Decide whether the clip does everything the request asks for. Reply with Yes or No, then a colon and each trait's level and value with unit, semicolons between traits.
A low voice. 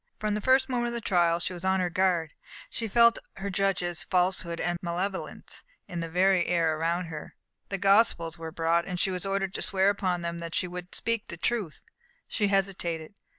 No: medium, 180 Hz